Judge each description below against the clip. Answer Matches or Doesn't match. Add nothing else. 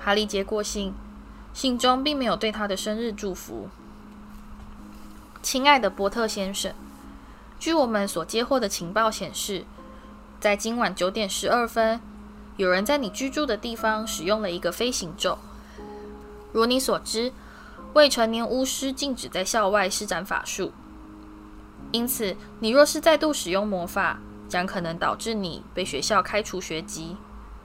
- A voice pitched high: Matches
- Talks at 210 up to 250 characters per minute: Matches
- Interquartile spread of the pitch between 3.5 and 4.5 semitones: Matches